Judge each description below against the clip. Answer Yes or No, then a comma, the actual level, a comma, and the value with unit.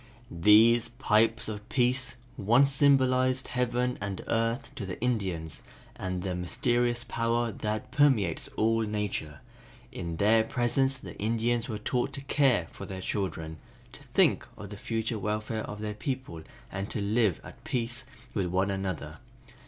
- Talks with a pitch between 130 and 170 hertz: No, low, 110 Hz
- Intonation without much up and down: No, average, 3.6 semitones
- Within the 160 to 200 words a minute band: No, average, 150 wpm